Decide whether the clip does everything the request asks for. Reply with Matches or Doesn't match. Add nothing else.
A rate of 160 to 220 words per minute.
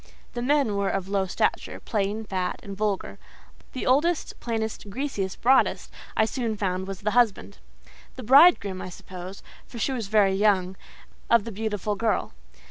Doesn't match